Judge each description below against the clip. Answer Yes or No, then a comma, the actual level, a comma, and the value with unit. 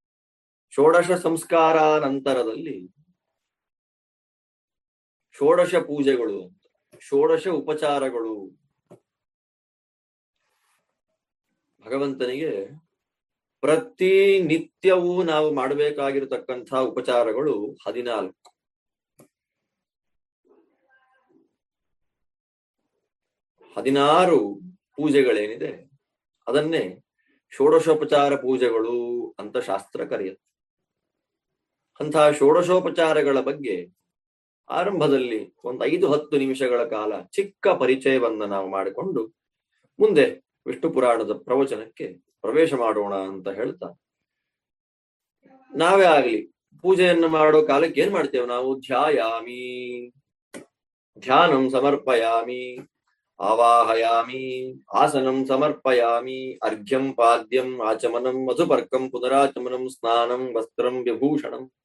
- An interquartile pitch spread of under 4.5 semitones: No, average, 5.2 semitones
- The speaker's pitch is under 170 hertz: Yes, low, 135 Hz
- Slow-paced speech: Yes, slow, 60 wpm